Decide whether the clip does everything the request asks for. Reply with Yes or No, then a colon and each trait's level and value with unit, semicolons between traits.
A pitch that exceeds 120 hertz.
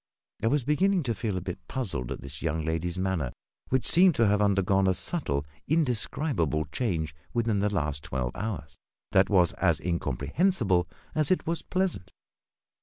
No: very low, 95 Hz